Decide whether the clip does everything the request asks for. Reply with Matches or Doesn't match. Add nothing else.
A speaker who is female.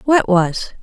Matches